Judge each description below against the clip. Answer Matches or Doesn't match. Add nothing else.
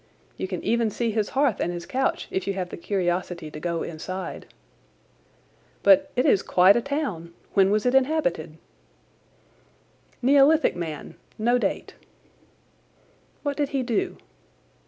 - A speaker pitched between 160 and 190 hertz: Doesn't match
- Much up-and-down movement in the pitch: Matches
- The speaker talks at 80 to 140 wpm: Matches